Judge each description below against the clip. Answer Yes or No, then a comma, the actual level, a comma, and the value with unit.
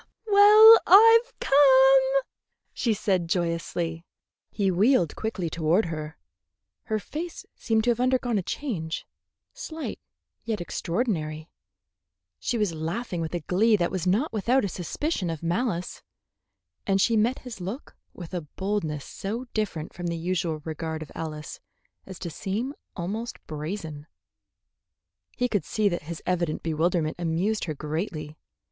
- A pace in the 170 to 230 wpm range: No, average, 140 wpm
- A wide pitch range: Yes, wide, 6.2 semitones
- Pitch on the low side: No, medium, 185 Hz